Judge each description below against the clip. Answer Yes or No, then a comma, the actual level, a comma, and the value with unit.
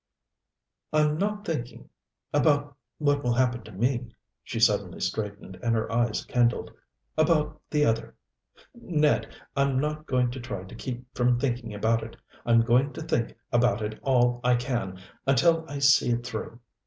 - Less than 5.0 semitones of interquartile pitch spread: Yes, average, 3.8 semitones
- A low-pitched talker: Yes, low, 125 Hz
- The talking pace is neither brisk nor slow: Yes, average, 160 wpm